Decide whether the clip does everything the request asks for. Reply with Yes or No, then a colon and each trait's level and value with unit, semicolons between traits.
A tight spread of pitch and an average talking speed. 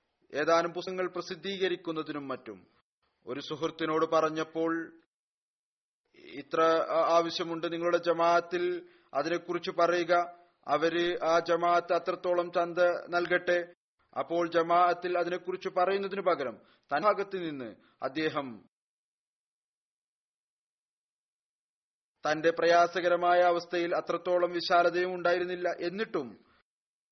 Yes: narrow, 1.3 semitones; average, 75 wpm